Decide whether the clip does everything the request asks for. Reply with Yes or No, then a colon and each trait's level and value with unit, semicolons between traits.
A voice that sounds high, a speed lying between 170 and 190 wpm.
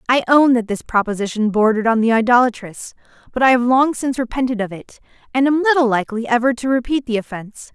No: high, 240 Hz; average, 200 wpm